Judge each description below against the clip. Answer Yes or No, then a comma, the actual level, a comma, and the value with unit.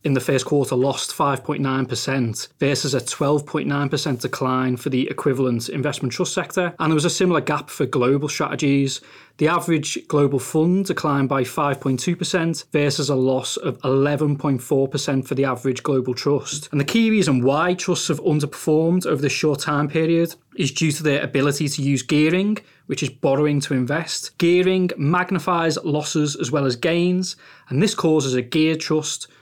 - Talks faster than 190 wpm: No, average, 165 wpm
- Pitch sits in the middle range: Yes, medium, 145 Hz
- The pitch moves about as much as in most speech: Yes, average, 3.1 semitones